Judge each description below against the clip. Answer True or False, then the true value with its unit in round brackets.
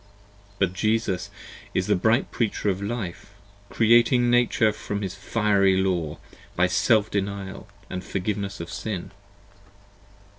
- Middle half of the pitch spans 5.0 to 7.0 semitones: False (2.7 semitones)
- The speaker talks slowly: True (120 wpm)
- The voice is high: False (100 Hz)